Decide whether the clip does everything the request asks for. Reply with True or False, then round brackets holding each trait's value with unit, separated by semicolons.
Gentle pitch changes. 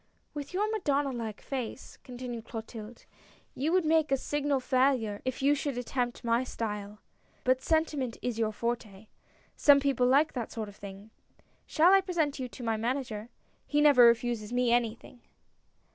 False (3.8 semitones)